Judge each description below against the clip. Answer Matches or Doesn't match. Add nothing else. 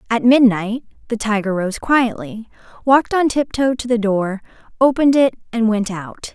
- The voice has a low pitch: Doesn't match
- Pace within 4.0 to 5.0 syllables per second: Matches